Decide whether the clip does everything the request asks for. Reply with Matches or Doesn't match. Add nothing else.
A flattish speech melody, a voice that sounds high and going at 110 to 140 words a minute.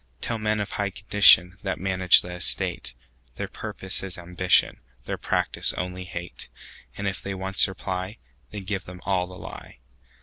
Doesn't match